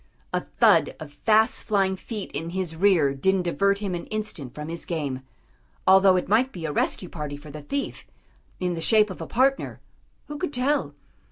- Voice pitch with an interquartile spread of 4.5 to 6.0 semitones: Yes, wide, 5.4 semitones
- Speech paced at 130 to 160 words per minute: No, average, 190 wpm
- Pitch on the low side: No, medium, 185 Hz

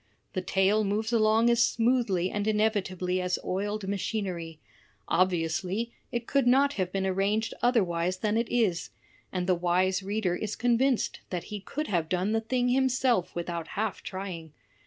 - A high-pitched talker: Yes, high, 200 Hz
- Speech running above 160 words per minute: No, average, 155 wpm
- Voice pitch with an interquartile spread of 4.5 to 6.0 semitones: No, average, 3.9 semitones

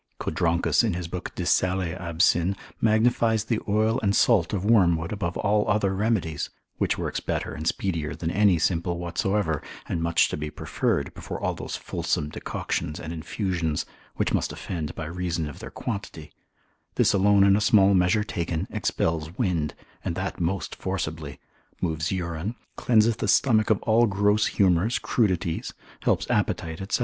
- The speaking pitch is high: No, very low, 95 Hz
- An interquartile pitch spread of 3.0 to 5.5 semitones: Yes, average, 4.0 semitones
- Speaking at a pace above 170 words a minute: No, average, 160 wpm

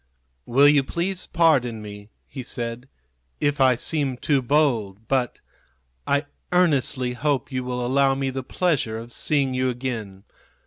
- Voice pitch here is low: Yes, low, 130 Hz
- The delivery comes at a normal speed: Yes, average, 145 wpm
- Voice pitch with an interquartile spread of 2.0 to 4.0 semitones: Yes, average, 3.0 semitones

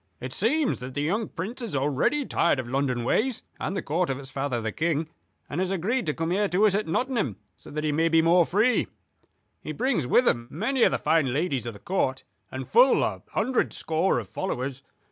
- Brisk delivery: Yes, fast, 220 wpm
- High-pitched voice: No, medium, 165 Hz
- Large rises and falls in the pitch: Yes, wide, 7.6 semitones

